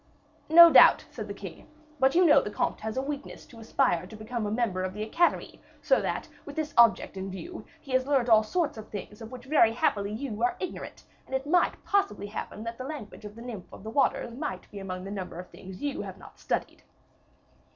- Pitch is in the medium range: No, high, 230 Hz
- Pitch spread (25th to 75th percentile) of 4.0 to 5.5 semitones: Yes, average, 5.1 semitones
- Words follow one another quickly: Yes, fast, 230 wpm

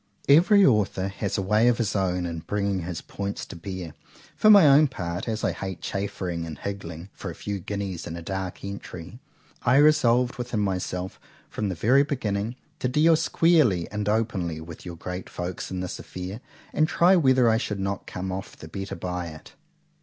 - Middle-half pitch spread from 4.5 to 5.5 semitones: Yes, average, 4.9 semitones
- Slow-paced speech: No, average, 185 wpm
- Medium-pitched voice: No, low, 100 Hz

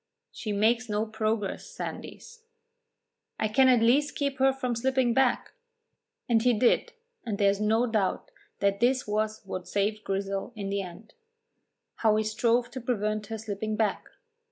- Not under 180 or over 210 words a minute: No, average, 160 wpm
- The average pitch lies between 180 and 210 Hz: No, high, 220 Hz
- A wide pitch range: No, average, 2.9 semitones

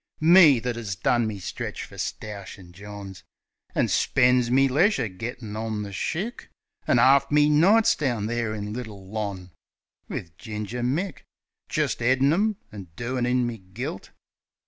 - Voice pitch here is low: Yes, low, 120 Hz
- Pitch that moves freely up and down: No, average, 4.3 semitones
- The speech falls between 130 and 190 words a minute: Yes, average, 150 wpm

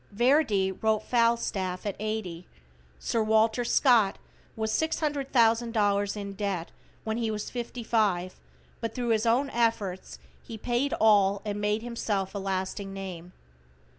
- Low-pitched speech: No, high, 215 Hz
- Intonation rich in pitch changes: No, average, 3.0 semitones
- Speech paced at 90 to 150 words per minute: Yes, slow, 135 wpm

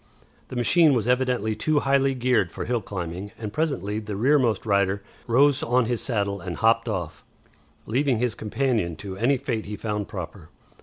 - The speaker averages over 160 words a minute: Yes, average, 170 wpm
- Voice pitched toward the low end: Yes, low, 110 Hz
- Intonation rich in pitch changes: No, average, 4.2 semitones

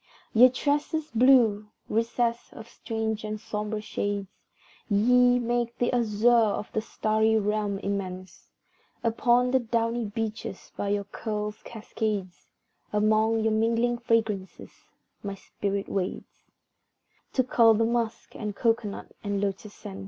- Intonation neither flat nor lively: No, narrow, 2.2 semitones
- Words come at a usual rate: No, slow, 130 wpm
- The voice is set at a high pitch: Yes, high, 220 Hz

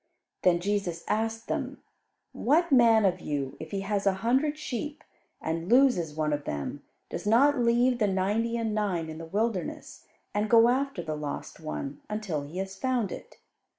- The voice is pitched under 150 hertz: No, high, 210 Hz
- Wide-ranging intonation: Yes, wide, 5.9 semitones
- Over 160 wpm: Yes, average, 175 wpm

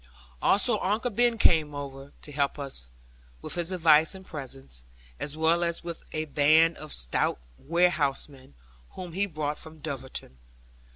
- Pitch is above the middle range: No, medium, 155 Hz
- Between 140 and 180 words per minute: Yes, average, 150 wpm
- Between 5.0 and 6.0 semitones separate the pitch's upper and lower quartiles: No, average, 3.5 semitones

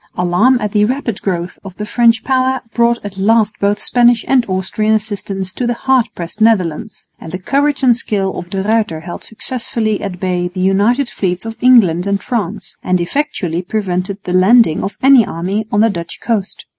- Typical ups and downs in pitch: Yes, average, 4.2 semitones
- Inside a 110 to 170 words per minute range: No, average, 190 wpm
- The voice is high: Yes, high, 210 Hz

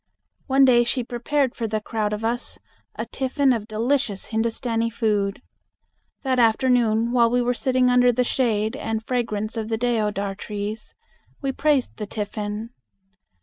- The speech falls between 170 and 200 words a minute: No, average, 150 wpm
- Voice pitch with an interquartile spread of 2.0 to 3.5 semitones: Yes, narrow, 2.6 semitones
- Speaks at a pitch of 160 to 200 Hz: No, high, 230 Hz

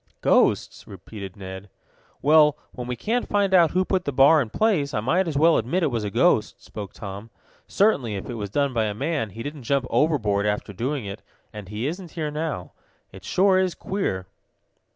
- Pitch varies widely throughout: Yes, wide, 7.8 semitones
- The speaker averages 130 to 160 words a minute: No, average, 200 wpm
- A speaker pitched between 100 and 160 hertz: Yes, low, 135 Hz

